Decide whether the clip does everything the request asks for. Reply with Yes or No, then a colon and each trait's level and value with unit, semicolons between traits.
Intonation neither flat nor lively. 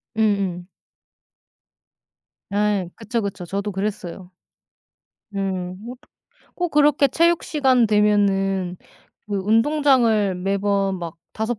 Yes: average, 3.3 semitones